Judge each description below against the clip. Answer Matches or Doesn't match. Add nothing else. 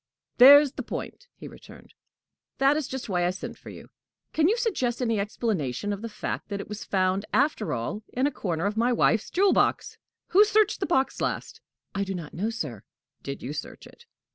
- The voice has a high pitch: Matches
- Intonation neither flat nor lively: Doesn't match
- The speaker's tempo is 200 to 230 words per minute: Matches